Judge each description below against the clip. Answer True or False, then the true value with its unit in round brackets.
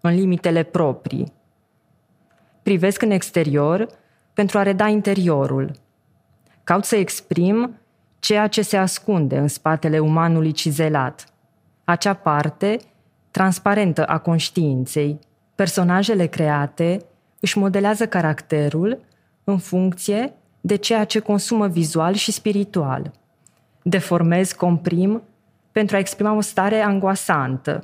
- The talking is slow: True (105 wpm)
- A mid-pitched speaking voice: True (180 Hz)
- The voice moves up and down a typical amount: True (4.4 semitones)